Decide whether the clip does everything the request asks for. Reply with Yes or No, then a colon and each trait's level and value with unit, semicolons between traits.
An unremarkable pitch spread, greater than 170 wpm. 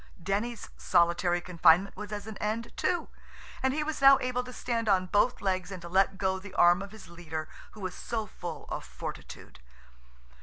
Yes: average, 4.4 semitones; average, 185 wpm